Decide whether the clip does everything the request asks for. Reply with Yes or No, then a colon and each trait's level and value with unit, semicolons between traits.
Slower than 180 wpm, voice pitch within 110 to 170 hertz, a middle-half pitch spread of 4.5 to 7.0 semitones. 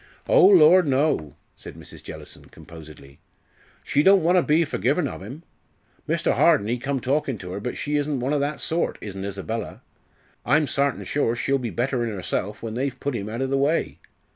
No: average, 195 wpm; low, 135 Hz; wide, 5.4 semitones